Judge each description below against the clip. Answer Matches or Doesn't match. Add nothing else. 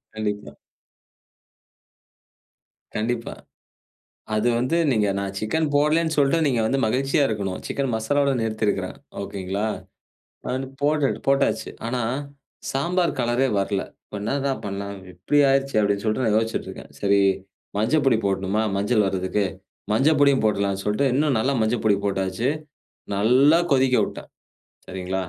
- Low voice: Matches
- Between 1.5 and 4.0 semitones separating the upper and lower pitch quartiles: Doesn't match